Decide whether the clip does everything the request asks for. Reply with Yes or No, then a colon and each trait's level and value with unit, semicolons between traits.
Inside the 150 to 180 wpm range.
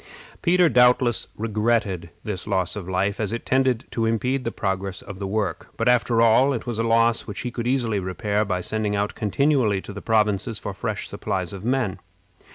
No: average, 195 wpm